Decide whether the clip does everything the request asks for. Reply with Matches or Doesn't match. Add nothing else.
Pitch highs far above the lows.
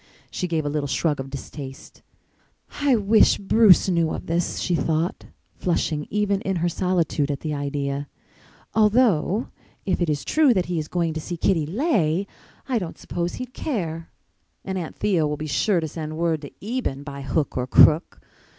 Doesn't match